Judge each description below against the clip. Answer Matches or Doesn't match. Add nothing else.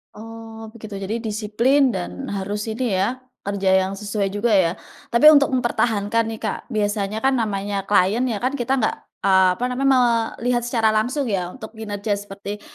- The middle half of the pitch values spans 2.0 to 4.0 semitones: Matches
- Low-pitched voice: Doesn't match